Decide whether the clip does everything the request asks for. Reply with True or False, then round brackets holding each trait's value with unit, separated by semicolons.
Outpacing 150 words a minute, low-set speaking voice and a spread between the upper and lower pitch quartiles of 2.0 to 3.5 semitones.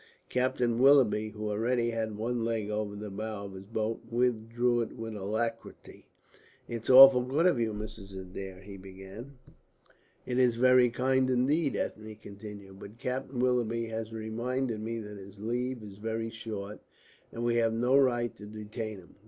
True (165 wpm; 115 Hz; 2.7 semitones)